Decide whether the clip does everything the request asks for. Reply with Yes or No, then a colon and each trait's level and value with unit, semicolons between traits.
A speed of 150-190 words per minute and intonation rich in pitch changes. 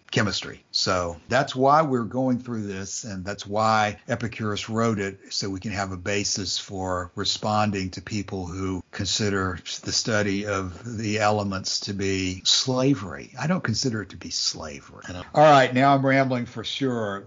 No: average, 165 wpm; average, 3.7 semitones